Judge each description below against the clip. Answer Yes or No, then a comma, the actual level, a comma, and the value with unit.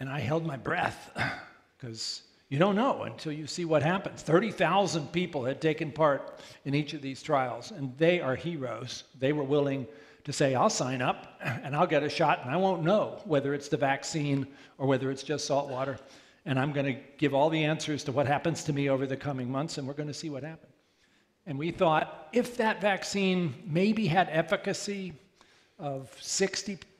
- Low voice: No, medium, 150 Hz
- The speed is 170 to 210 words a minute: Yes, average, 200 wpm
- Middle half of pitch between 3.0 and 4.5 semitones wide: Yes, average, 3.8 semitones